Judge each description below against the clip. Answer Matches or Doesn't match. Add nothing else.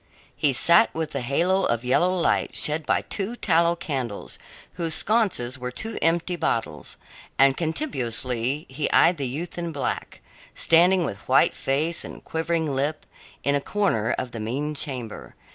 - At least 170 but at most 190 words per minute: Doesn't match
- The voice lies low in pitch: Doesn't match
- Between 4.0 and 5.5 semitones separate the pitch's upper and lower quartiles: Matches